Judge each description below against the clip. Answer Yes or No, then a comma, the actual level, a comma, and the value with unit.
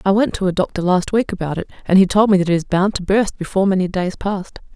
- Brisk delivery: Yes, fast, 290 wpm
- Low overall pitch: No, high, 190 Hz